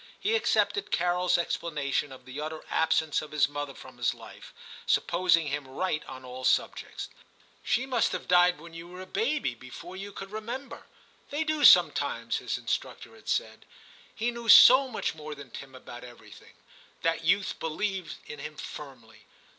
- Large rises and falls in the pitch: Yes, wide, 6.1 semitones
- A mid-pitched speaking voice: Yes, medium, 165 Hz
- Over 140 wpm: Yes, average, 170 wpm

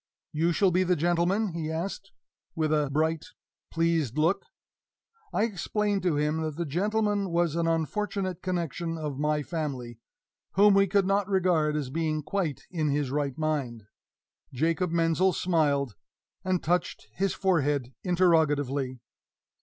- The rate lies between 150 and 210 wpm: No, average, 140 wpm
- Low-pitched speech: No, medium, 165 Hz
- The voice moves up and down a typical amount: Yes, average, 3.7 semitones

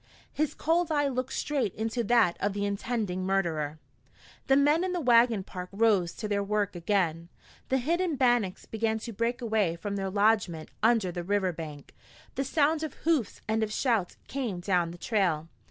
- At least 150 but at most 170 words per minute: No, average, 180 wpm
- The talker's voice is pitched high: Yes, high, 215 Hz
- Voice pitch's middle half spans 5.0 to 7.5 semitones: Yes, average, 5.3 semitones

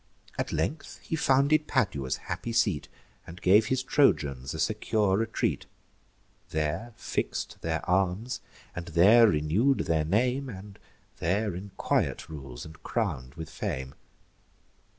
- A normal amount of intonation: No, wide, 6.8 semitones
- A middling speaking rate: No, slow, 130 wpm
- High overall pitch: No, very low, 95 Hz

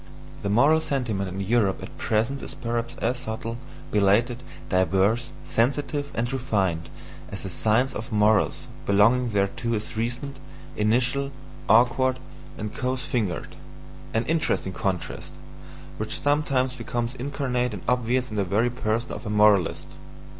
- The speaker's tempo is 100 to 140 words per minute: Yes, slow, 135 wpm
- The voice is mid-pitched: No, low, 115 Hz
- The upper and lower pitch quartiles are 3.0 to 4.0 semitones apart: Yes, average, 3.5 semitones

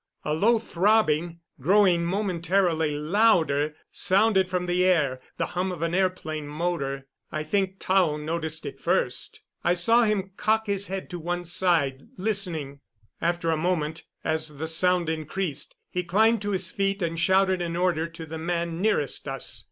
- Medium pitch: Yes, medium, 175 Hz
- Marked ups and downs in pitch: No, average, 3.2 semitones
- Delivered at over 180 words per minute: No, average, 160 wpm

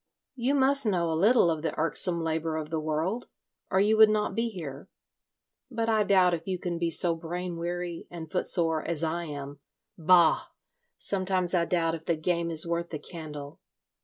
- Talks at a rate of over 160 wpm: Yes, average, 190 wpm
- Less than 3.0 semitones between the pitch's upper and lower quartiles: Yes, narrow, 2.6 semitones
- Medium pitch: Yes, medium, 170 Hz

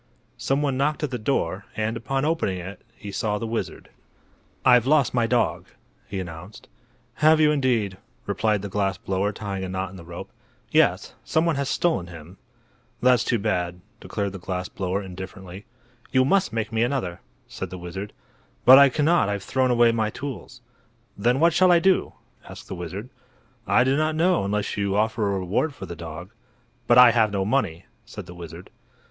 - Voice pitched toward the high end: No, low, 110 Hz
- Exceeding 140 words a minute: Yes, average, 190 wpm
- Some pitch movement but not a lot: No, wide, 5.7 semitones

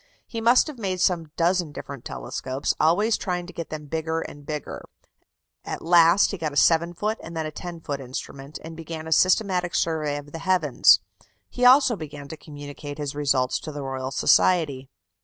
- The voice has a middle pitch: Yes, medium, 160 Hz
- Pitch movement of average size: Yes, average, 3.7 semitones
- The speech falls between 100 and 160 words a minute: No, average, 190 wpm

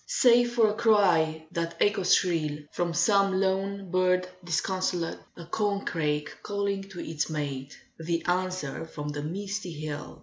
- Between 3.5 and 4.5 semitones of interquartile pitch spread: Yes, average, 3.8 semitones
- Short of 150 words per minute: Yes, average, 140 wpm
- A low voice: No, medium, 180 Hz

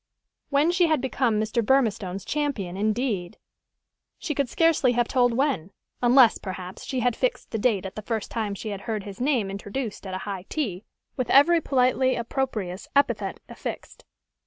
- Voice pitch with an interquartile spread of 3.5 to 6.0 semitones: Yes, average, 5.2 semitones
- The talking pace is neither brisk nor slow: Yes, average, 170 wpm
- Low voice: No, high, 235 Hz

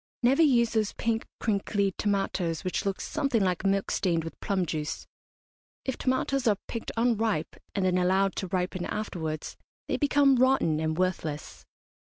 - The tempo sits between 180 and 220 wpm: No, average, 155 wpm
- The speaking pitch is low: No, high, 195 Hz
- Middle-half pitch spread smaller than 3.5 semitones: No, average, 4.5 semitones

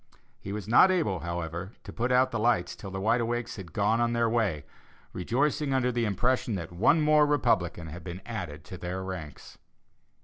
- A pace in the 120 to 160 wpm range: No, average, 195 wpm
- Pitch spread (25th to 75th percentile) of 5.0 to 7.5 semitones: Yes, wide, 5.4 semitones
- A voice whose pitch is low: Yes, low, 110 Hz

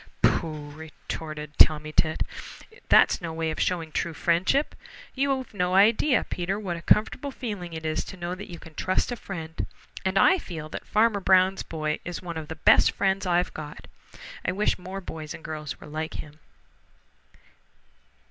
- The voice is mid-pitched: Yes, medium, 175 Hz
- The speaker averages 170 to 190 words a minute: Yes, average, 175 wpm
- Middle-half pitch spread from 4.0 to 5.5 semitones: No, average, 3.6 semitones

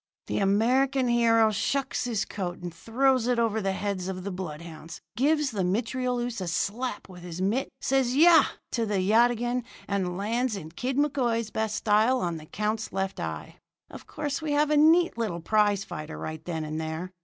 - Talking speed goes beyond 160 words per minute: Yes, average, 185 wpm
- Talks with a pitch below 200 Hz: No, high, 220 Hz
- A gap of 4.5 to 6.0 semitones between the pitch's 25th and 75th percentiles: Yes, average, 5.1 semitones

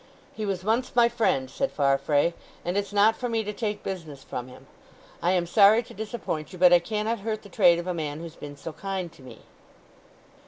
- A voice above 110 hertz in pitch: Yes, medium, 185 Hz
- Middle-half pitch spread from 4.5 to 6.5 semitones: Yes, average, 5.2 semitones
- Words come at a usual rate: No, fast, 220 wpm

